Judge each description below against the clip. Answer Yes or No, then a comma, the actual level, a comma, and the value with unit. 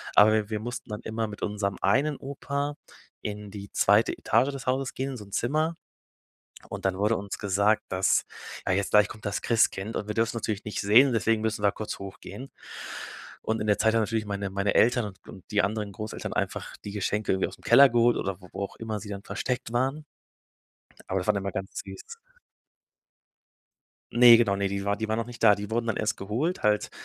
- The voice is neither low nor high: No, low, 105 Hz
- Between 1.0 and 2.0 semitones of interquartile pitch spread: No, average, 2.7 semitones